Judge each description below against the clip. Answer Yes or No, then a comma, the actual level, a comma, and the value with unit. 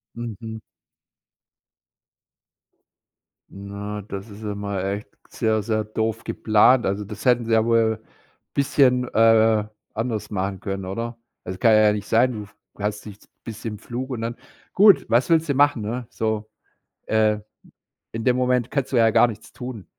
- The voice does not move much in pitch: Yes, narrow, 2.3 semitones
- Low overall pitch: Yes, low, 110 Hz